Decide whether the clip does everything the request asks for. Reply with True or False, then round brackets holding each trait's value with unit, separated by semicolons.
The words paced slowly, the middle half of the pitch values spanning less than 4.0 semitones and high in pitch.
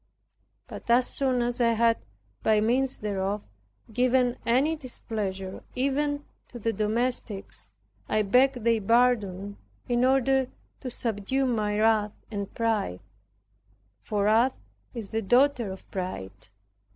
True (125 wpm; 3.5 semitones; 230 Hz)